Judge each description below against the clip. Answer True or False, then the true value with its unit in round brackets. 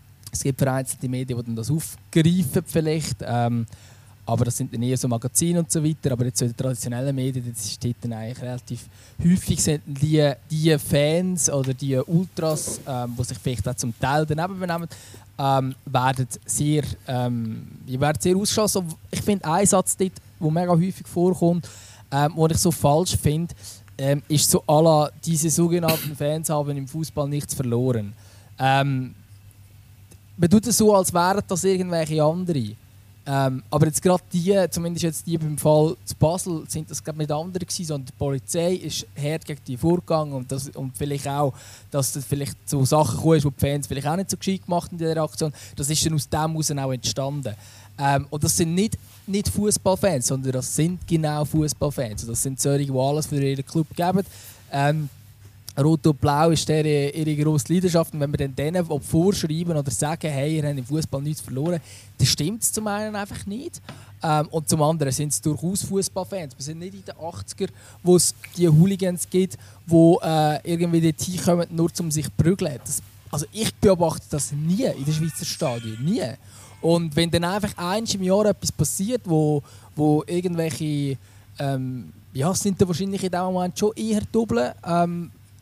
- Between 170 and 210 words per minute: True (185 wpm)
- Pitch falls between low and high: True (150 Hz)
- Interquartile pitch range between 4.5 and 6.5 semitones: True (4.8 semitones)